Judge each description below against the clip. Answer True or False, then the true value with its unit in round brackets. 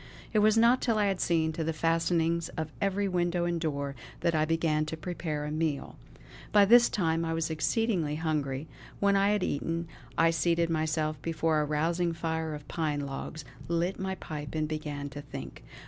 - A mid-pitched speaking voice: True (165 Hz)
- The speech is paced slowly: False (190 wpm)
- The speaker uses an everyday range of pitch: False (2.3 semitones)